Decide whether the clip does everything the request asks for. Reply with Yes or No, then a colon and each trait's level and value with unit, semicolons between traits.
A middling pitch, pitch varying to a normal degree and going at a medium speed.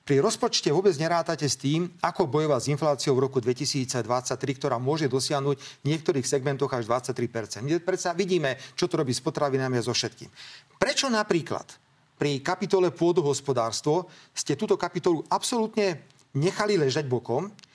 Yes: medium, 145 Hz; average, 5.0 semitones; average, 150 wpm